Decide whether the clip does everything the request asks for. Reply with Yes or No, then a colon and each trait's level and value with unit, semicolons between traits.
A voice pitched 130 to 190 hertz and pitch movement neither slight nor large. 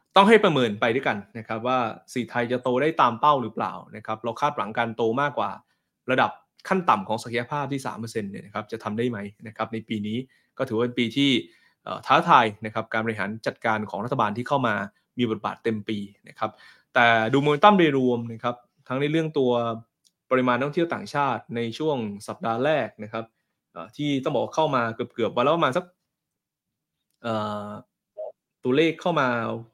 No: low, 120 Hz; average, 3.9 semitones